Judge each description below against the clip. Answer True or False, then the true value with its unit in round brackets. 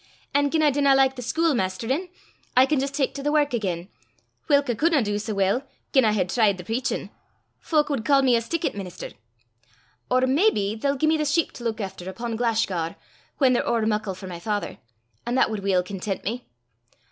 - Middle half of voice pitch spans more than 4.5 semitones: True (5.6 semitones)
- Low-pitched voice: False (240 Hz)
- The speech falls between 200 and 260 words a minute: True (205 wpm)